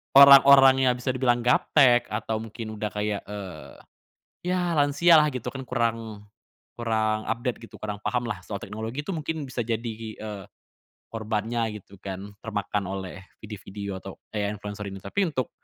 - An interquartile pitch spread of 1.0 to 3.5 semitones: No, average, 3.9 semitones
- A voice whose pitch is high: No, low, 110 Hz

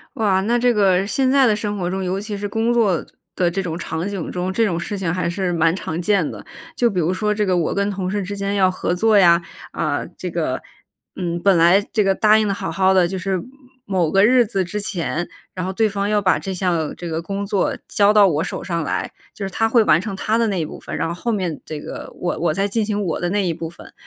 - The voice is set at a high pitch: Yes, high, 195 Hz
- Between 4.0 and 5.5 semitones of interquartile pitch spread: No, average, 2.9 semitones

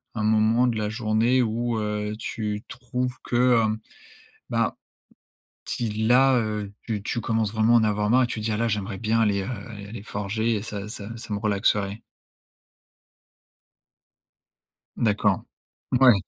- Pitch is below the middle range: Yes, low, 110 Hz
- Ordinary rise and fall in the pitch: No, narrow, 1.9 semitones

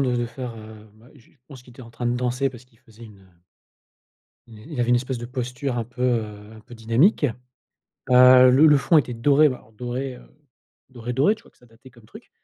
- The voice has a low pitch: Yes, low, 125 Hz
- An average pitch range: No, narrow, 2.0 semitones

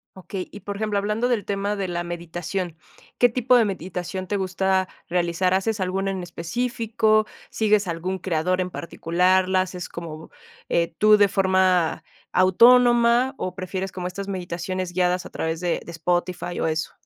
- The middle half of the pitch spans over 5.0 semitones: No, narrow, 2.6 semitones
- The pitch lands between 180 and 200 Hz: Yes, medium, 185 Hz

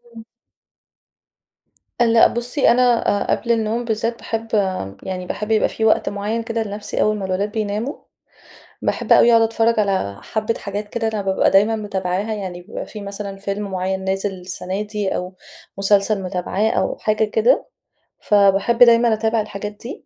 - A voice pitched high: Yes, high, 210 Hz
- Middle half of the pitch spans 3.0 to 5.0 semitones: No, narrow, 2.4 semitones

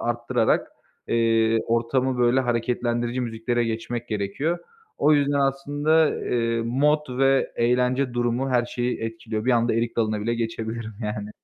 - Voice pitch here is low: Yes, low, 120 Hz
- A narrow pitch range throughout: Yes, narrow, 2.2 semitones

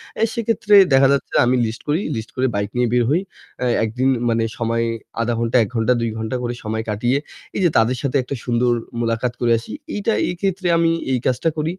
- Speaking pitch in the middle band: No, low, 125 Hz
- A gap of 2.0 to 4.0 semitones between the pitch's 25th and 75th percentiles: No, average, 4.7 semitones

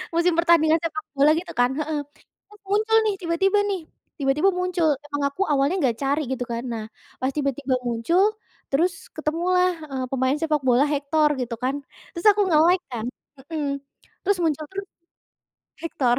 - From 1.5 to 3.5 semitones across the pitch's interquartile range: No, average, 4.4 semitones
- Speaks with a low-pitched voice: No, very high, 305 Hz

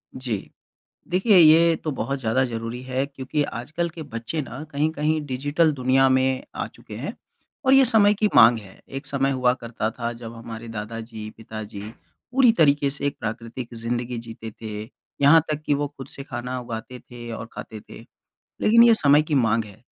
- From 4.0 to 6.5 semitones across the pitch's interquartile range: Yes, average, 4.4 semitones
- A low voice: Yes, low, 130 Hz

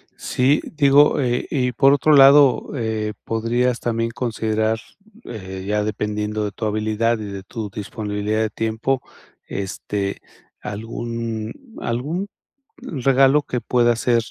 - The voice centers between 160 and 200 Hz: No, low, 115 Hz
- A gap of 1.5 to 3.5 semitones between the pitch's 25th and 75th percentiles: Yes, average, 2.9 semitones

